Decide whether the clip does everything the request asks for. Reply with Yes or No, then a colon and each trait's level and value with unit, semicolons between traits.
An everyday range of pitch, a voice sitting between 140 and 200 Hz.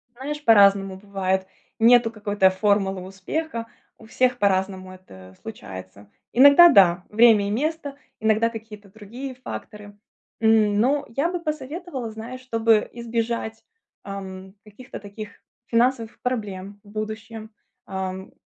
No: average, 3.6 semitones; high, 220 Hz